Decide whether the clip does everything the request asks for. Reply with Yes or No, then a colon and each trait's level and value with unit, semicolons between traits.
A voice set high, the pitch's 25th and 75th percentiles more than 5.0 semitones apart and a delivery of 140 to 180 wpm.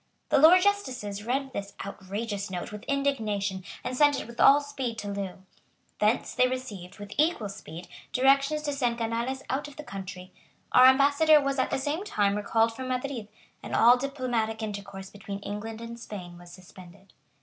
Yes: high, 230 Hz; wide, 5.4 semitones; average, 175 wpm